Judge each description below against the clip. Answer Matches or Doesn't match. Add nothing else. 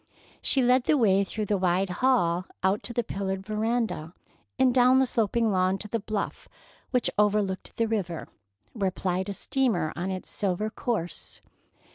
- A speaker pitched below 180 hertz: Doesn't match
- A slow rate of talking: Doesn't match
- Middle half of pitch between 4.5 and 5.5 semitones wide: Doesn't match